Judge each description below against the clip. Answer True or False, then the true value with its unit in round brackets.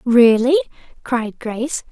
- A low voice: False (240 Hz)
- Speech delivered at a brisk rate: False (95 wpm)